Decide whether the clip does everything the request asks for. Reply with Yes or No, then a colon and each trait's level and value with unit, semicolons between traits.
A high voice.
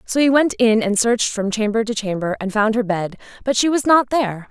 Yes: high, 225 Hz